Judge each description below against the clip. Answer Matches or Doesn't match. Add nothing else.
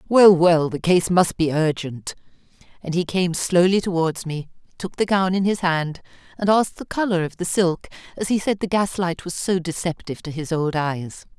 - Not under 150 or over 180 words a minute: Doesn't match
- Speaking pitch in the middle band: Matches